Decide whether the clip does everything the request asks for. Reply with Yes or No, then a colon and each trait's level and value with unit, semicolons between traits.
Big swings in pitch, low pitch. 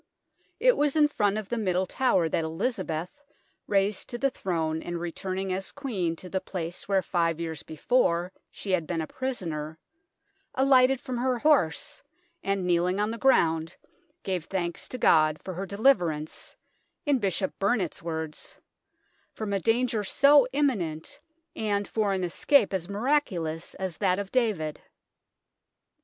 No: wide, 6.2 semitones; high, 190 Hz